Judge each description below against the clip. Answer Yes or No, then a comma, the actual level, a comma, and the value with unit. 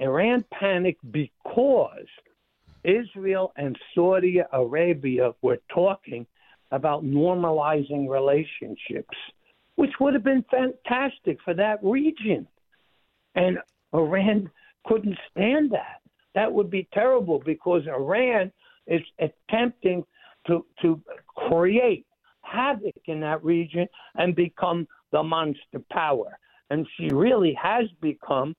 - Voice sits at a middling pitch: Yes, medium, 180 Hz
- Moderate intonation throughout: No, wide, 5.9 semitones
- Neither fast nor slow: No, slow, 105 wpm